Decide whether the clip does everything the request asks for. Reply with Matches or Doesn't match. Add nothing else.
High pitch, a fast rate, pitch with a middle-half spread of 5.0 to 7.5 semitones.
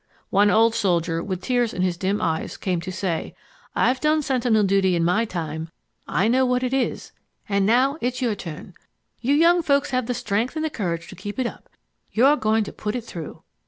Matches